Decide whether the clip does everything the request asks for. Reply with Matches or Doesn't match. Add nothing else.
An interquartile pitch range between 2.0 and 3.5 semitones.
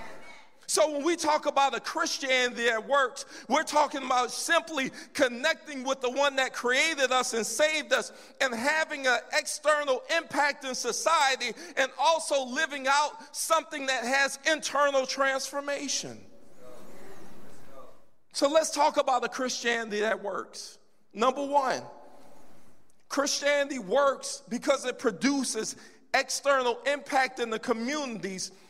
Matches